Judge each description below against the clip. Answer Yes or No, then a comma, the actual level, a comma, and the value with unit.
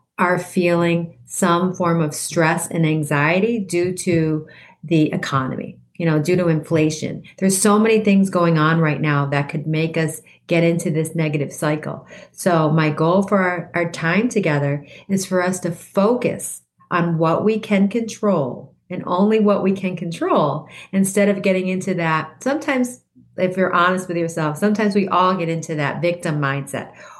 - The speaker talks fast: No, average, 170 wpm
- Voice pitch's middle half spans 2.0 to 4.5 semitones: Yes, average, 3.3 semitones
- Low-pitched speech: No, medium, 175 Hz